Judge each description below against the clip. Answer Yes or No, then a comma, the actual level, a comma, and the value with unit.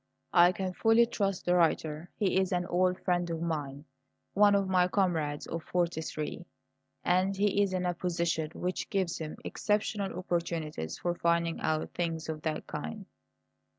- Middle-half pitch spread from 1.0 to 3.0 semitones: Yes, narrow, 2.5 semitones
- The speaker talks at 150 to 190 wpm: Yes, average, 160 wpm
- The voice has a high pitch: No, medium, 175 Hz